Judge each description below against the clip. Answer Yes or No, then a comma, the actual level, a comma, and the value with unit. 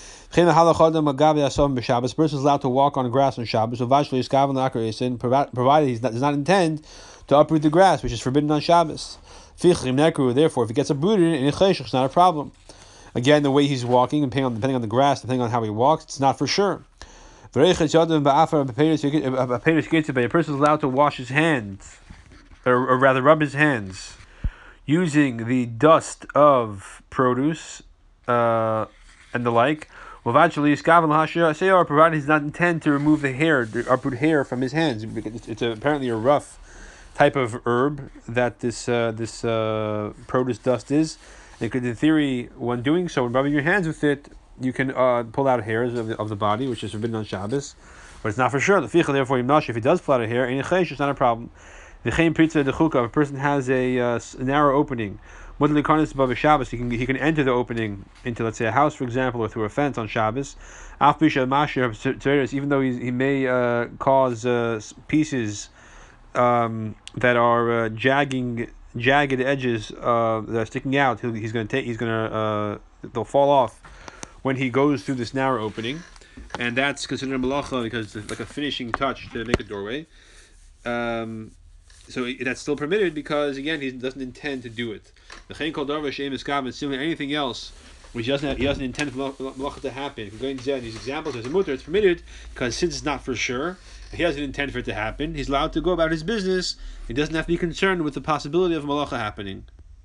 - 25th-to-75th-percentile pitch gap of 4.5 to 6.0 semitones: No, average, 3.8 semitones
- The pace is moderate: Yes, average, 190 wpm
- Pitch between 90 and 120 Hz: No, low, 135 Hz